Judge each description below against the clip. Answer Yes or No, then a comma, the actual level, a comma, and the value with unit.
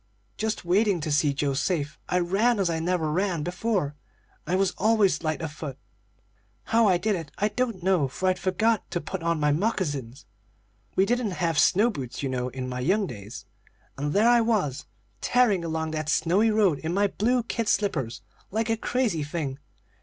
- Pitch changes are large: Yes, wide, 6.0 semitones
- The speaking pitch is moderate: Yes, medium, 180 Hz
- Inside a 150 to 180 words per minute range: No, average, 190 wpm